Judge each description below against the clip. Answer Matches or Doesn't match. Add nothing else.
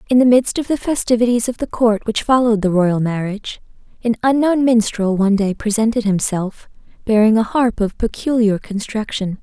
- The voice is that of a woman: Matches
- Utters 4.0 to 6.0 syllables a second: Matches